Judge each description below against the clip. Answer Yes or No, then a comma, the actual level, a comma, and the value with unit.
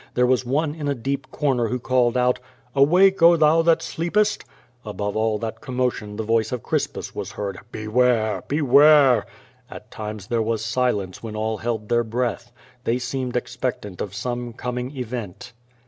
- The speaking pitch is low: Yes, low, 120 Hz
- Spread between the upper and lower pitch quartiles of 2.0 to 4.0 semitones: Yes, average, 3.5 semitones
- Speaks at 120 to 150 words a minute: No, average, 165 wpm